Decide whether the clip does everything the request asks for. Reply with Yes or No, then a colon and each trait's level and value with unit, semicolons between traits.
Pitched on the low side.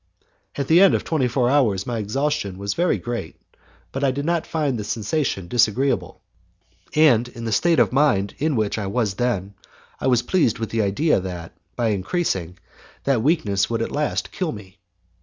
Yes: low, 120 Hz